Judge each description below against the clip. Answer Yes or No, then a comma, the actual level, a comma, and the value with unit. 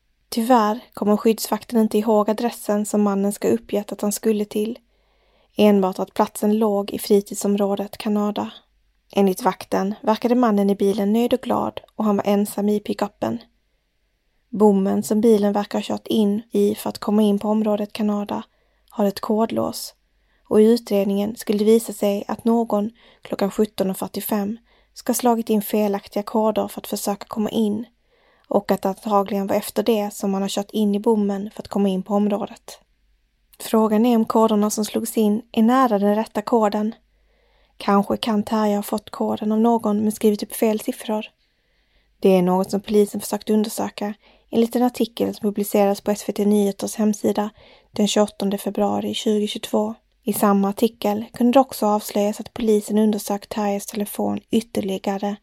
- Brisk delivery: No, average, 170 wpm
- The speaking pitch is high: Yes, high, 210 Hz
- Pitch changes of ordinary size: No, narrow, 1.7 semitones